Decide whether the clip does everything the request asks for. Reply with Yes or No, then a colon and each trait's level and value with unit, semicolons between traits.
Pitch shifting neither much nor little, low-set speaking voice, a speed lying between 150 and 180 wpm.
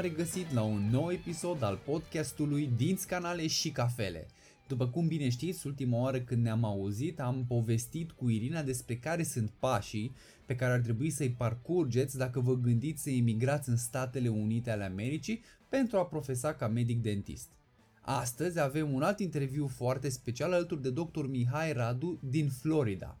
Yes: average, 4.8 semitones; low, 130 Hz; average, 165 wpm